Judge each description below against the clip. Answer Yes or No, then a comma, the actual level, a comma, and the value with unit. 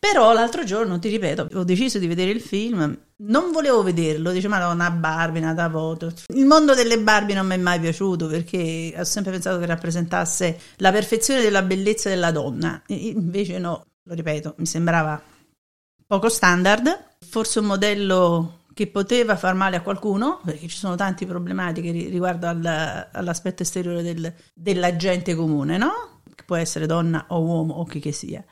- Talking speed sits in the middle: No, fast, 175 wpm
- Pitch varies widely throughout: No, average, 3.5 semitones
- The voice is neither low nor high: Yes, medium, 180 Hz